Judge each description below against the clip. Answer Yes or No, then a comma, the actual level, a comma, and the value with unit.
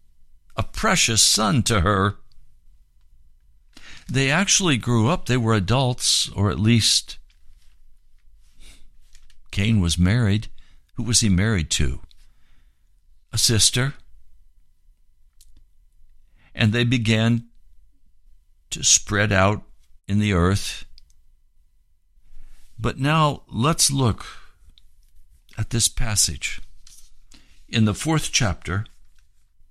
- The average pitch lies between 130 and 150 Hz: No, very low, 90 Hz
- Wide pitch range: Yes, wide, 8.1 semitones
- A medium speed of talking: No, slow, 90 wpm